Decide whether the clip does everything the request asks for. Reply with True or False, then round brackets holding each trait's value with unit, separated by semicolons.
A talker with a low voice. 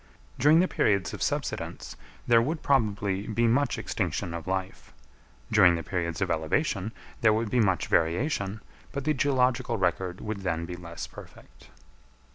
True (100 Hz)